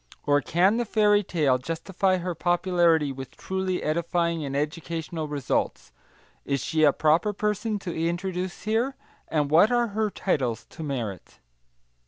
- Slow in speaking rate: No, average, 145 wpm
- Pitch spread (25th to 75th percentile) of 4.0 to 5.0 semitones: Yes, average, 4.5 semitones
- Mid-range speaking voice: Yes, medium, 170 Hz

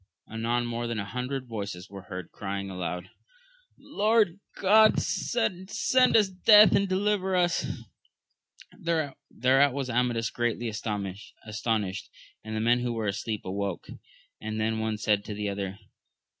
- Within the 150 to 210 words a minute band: No, slow, 135 wpm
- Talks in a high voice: No, low, 115 Hz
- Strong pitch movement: Yes, wide, 8.6 semitones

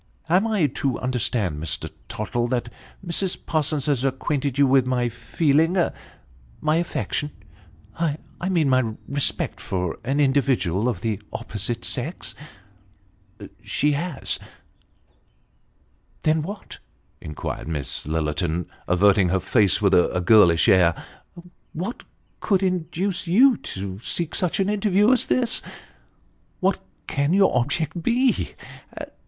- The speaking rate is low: Yes, slow, 130 wpm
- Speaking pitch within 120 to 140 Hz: Yes, low, 135 Hz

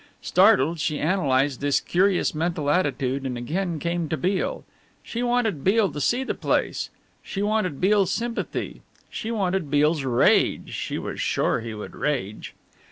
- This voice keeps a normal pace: Yes, average, 155 wpm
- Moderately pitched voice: Yes, medium, 165 Hz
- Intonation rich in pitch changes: Yes, wide, 5.8 semitones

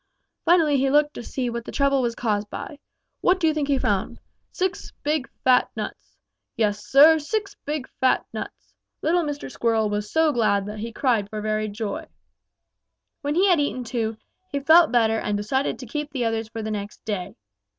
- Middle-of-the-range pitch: No, very high, 250 Hz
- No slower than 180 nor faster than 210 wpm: Yes, average, 190 wpm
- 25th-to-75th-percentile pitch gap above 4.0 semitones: Yes, wide, 5.5 semitones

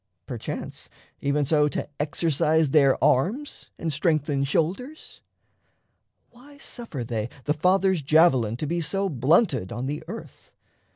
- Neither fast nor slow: No, slow, 125 wpm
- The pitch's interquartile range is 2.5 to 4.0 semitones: No, average, 5.0 semitones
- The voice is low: No, medium, 155 Hz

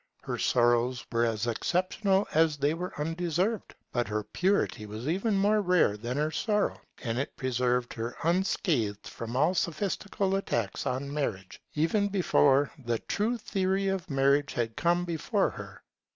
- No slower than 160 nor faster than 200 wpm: No, average, 150 wpm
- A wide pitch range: Yes, wide, 7.7 semitones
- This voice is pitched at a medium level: Yes, medium, 150 Hz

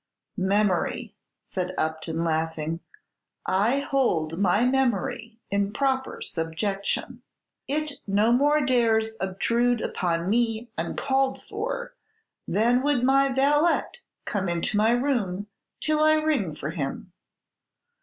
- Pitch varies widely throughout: Yes, wide, 6.7 semitones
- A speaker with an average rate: No, slow, 110 wpm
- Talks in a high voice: Yes, high, 225 Hz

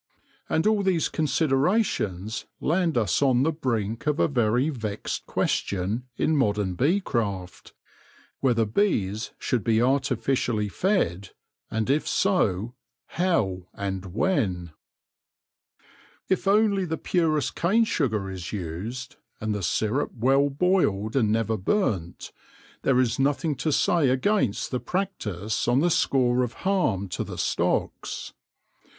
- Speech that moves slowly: Yes, slow, 130 wpm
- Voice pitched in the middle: No, low, 125 Hz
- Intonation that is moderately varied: No, wide, 7.4 semitones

